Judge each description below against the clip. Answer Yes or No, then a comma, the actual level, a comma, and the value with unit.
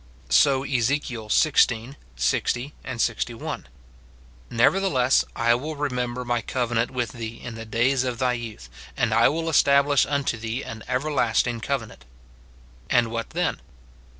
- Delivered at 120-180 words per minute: Yes, slow, 135 wpm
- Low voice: Yes, low, 125 Hz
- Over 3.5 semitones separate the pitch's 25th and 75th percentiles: No, average, 3.2 semitones